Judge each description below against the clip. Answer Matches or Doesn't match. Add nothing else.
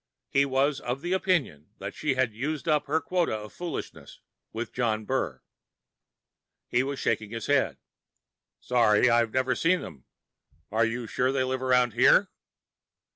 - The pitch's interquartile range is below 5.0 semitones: Matches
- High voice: Doesn't match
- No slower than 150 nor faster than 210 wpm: Matches